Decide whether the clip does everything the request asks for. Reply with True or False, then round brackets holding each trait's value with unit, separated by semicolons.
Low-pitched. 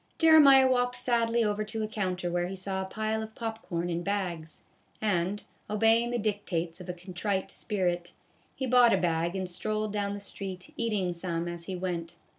False (200 Hz)